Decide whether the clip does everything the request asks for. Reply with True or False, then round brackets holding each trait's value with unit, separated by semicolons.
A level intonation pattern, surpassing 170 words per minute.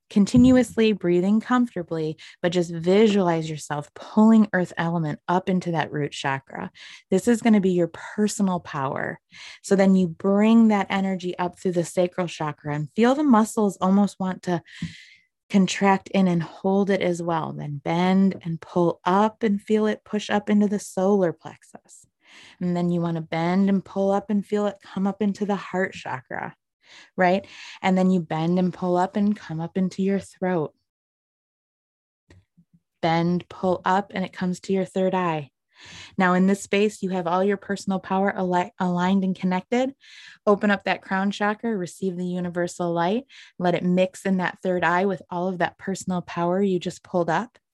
True (2.3 semitones; 180 wpm)